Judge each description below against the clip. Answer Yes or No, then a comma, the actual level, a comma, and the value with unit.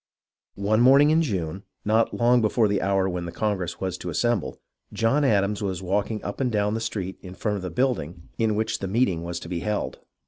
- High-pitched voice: No, low, 105 Hz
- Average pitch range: Yes, average, 3.4 semitones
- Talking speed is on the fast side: Yes, fast, 215 wpm